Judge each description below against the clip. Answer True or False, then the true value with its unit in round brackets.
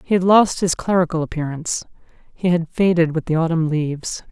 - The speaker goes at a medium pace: True (165 wpm)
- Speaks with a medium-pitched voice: True (170 Hz)